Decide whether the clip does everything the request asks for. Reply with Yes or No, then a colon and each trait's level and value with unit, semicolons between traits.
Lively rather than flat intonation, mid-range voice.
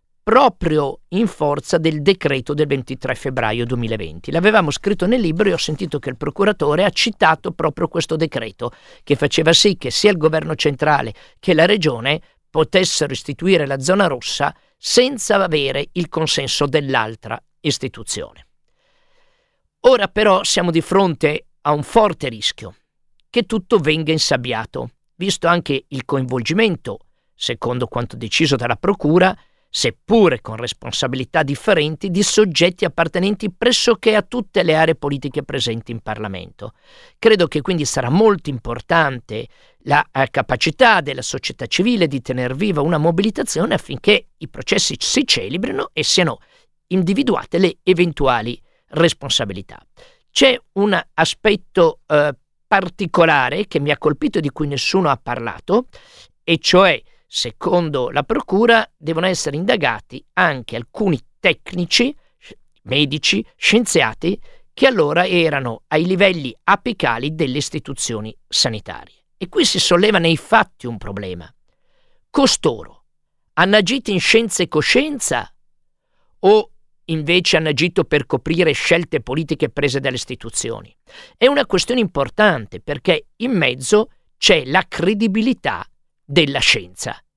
Yes: wide, 6.5 semitones; medium, 165 Hz